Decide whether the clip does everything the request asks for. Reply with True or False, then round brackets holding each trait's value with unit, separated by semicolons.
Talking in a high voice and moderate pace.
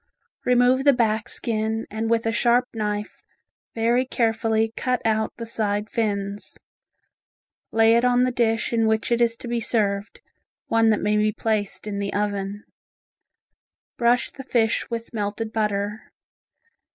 True (225 Hz; 150 wpm)